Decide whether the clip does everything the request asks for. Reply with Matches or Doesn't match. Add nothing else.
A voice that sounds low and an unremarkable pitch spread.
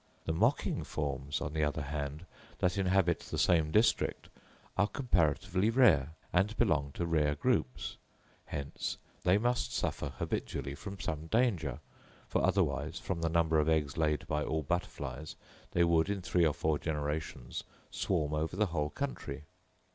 Matches